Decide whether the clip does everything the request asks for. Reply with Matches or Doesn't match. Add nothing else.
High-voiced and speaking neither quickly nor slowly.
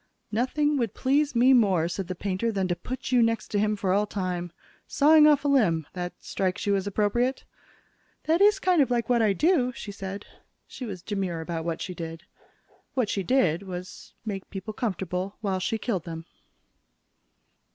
Matches